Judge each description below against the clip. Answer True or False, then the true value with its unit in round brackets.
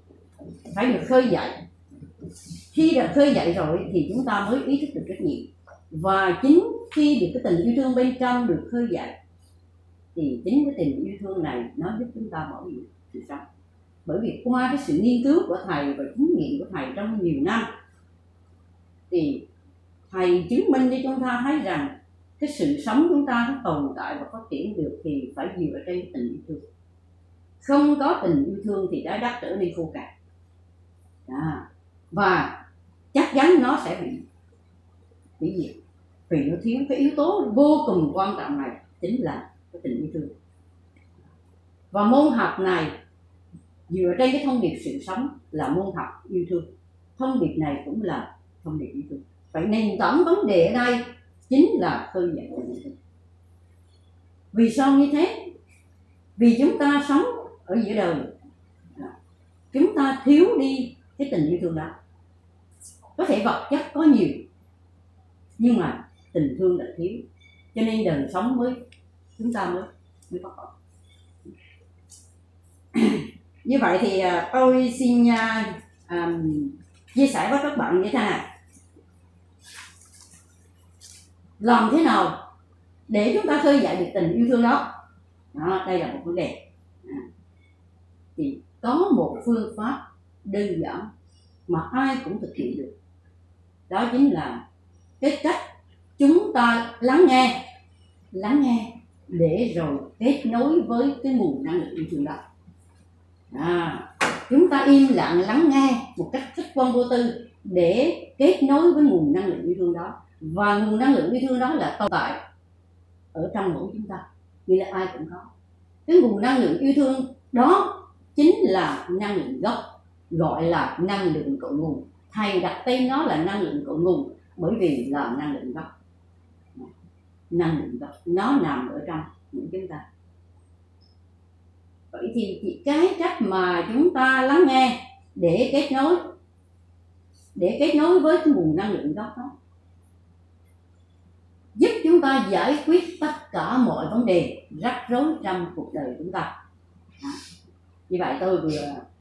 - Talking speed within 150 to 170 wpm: True (165 wpm)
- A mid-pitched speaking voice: True (180 Hz)